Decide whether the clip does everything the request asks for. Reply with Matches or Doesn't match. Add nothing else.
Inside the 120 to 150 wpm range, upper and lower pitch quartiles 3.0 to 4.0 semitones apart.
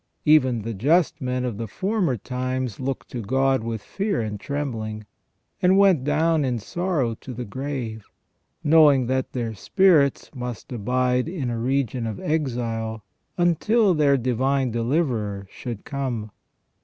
Doesn't match